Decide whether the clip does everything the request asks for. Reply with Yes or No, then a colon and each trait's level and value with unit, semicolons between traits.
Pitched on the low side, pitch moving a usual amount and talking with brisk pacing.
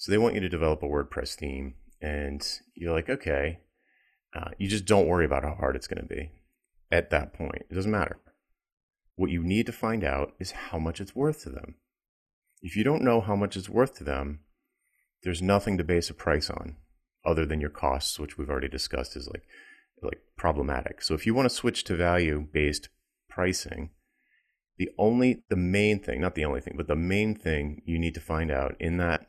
Yes: very low, 85 Hz; average, 4.8 semitones; fast, 210 wpm